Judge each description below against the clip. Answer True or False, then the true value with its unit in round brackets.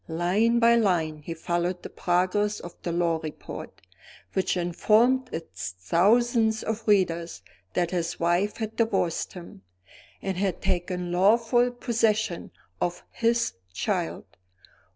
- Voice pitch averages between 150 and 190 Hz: True (185 Hz)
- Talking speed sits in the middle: False (125 wpm)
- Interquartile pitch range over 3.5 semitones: True (4.5 semitones)